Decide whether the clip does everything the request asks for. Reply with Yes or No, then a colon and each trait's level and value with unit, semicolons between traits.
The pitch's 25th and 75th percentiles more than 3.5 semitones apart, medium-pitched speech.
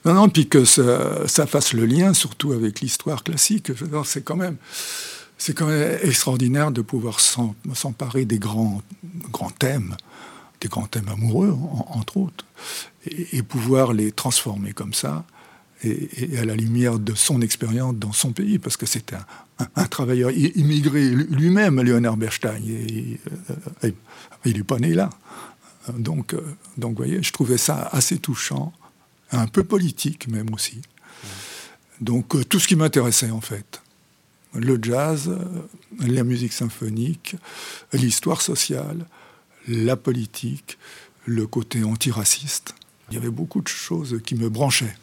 No: wide, 5.4 semitones; low, 130 Hz